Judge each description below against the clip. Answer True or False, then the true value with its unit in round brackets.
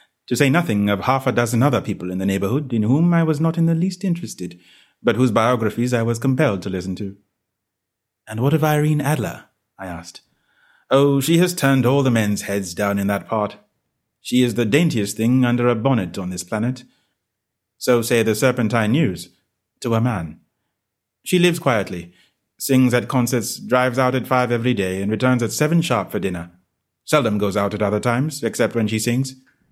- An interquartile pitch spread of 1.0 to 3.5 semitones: False (4.4 semitones)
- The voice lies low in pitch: True (120 Hz)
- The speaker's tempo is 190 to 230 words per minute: True (195 wpm)